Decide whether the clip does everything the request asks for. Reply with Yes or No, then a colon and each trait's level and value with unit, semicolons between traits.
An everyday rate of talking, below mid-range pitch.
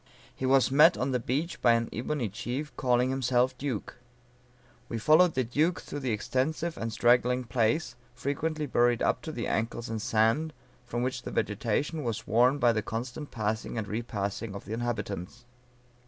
Yes: average, 170 wpm; low, 125 Hz